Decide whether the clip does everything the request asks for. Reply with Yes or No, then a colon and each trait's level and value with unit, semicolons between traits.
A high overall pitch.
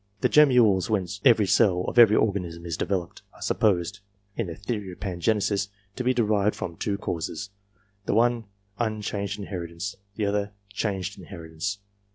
No: low, 100 Hz